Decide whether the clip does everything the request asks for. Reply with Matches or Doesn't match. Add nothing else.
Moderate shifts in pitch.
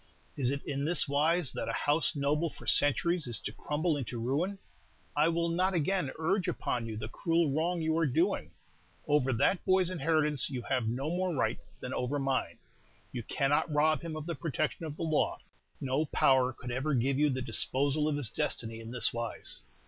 Matches